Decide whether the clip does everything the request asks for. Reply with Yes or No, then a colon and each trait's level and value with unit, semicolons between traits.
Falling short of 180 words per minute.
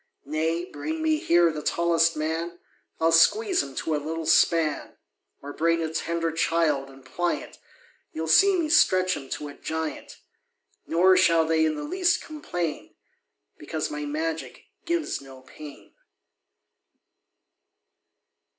Yes: slow, 135 wpm